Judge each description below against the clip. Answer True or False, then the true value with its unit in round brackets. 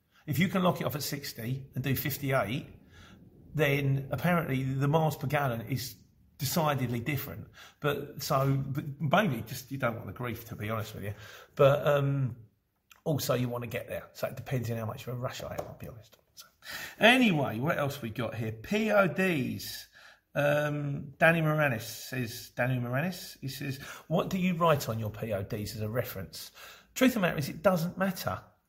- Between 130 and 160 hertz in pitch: True (135 Hz)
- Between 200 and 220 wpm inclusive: False (190 wpm)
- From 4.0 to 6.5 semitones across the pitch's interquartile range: True (4.4 semitones)